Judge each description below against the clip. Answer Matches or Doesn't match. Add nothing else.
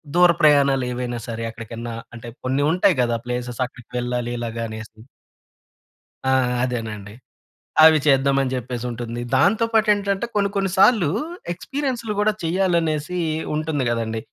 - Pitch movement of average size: Doesn't match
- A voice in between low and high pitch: Doesn't match